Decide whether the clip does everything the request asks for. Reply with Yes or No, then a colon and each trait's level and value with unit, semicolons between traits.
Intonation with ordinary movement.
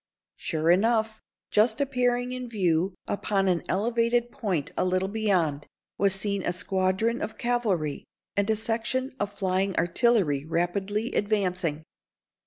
Yes: average, 4.0 semitones